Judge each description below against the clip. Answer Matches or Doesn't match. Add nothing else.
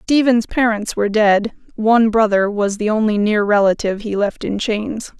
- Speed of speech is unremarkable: Matches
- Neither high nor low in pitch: Doesn't match